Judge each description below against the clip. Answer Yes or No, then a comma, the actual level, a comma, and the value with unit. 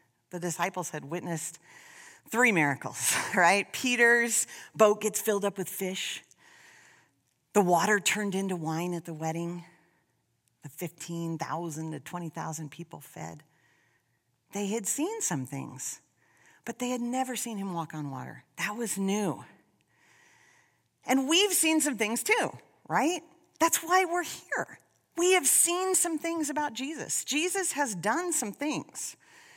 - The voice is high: Yes, high, 210 Hz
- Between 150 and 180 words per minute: No, average, 140 wpm